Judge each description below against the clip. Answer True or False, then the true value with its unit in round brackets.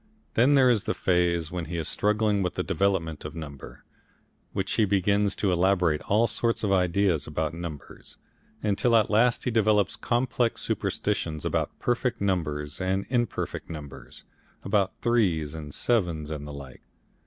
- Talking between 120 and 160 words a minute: True (155 wpm)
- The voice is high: False (95 Hz)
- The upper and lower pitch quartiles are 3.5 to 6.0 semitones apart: True (5.2 semitones)